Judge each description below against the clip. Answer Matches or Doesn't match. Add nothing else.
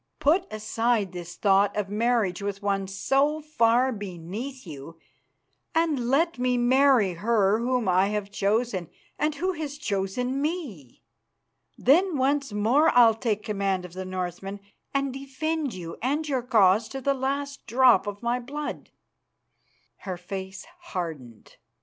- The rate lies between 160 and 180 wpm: Doesn't match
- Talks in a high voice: Matches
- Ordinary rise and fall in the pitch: Doesn't match